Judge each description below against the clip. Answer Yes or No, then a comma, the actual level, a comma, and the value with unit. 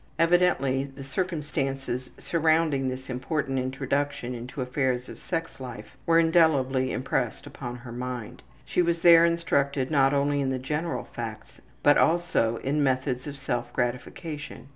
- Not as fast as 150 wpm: Yes, average, 140 wpm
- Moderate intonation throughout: Yes, average, 3.7 semitones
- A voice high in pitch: No, low, 135 Hz